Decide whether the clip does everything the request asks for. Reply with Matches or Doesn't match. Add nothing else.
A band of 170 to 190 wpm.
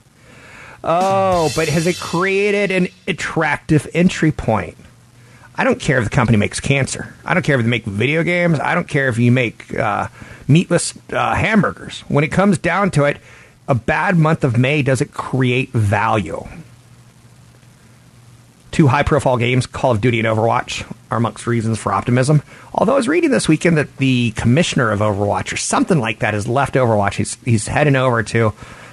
Matches